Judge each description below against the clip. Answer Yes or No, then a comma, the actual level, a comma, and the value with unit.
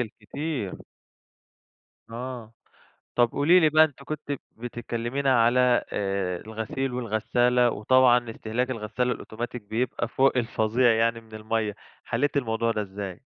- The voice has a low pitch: Yes, low, 120 Hz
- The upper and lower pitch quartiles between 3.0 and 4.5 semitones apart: No, narrow, 2.6 semitones